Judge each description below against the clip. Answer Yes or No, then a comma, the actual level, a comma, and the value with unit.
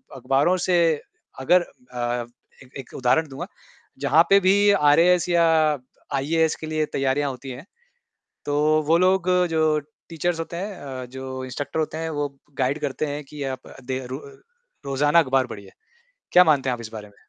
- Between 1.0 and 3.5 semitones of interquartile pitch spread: No, average, 3.9 semitones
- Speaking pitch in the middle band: Yes, medium, 145 Hz